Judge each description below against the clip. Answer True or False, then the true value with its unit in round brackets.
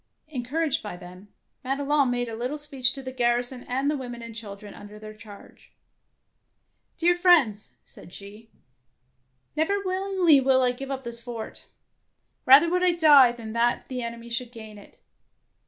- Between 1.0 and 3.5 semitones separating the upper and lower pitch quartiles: False (4.0 semitones)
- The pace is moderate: True (165 wpm)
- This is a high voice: True (250 Hz)